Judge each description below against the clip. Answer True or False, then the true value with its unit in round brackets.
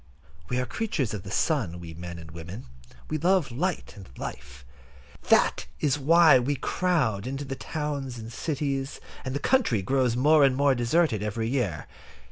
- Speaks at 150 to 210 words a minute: True (170 wpm)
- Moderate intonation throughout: False (5.8 semitones)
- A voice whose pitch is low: True (130 Hz)